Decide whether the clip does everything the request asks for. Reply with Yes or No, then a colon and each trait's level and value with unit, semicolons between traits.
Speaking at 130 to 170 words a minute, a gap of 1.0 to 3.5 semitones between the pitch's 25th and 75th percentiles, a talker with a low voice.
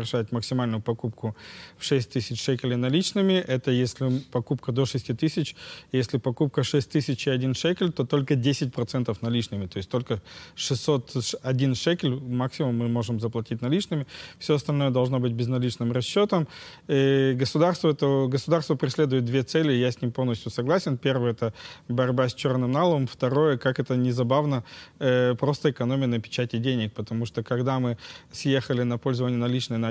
Yes: average, 155 wpm; average, 2.8 semitones; low, 130 Hz